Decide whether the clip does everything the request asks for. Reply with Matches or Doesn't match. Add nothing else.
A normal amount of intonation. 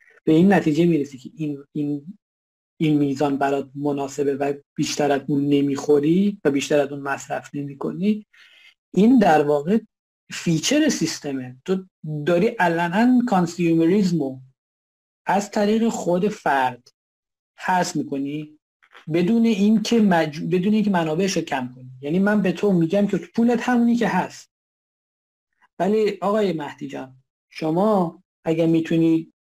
Doesn't match